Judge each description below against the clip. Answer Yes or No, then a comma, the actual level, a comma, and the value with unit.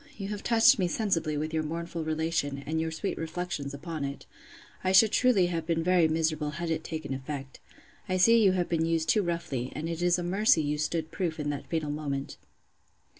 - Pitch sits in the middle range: Yes, medium, 165 Hz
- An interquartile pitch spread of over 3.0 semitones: No, average, 2.7 semitones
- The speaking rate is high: Yes, fast, 210 wpm